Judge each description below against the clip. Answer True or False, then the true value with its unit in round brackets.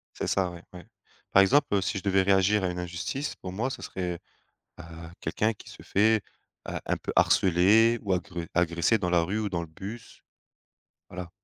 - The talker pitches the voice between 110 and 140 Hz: False (95 Hz)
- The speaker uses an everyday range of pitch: True (3.2 semitones)